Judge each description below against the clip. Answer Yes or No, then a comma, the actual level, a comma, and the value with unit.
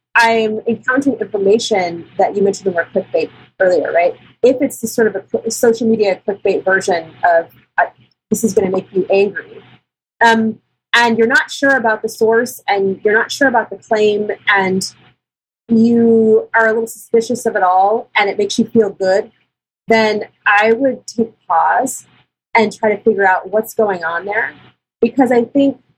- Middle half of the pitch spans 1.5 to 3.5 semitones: Yes, narrow, 2.6 semitones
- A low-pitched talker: No, high, 220 Hz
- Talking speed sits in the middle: Yes, average, 180 wpm